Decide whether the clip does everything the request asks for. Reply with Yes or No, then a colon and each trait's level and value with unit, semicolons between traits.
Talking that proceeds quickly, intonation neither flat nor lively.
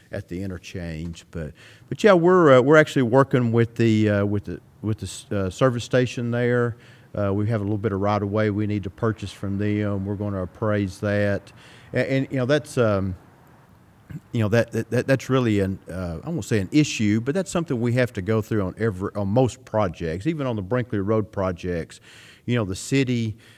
Yes: fast, 220 wpm; average, 3.9 semitones